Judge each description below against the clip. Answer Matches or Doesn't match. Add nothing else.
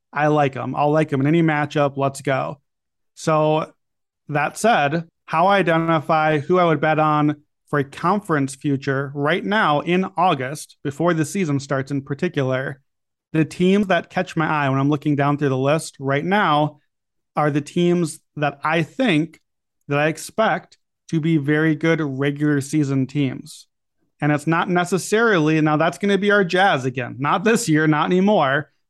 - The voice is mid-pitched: Matches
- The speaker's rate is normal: Matches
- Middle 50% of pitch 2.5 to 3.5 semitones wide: Matches